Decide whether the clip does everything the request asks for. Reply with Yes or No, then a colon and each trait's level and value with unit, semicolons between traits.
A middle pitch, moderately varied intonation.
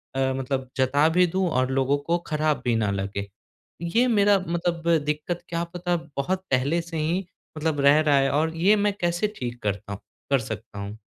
Yes: medium, 150 Hz; average, 4.9 semitones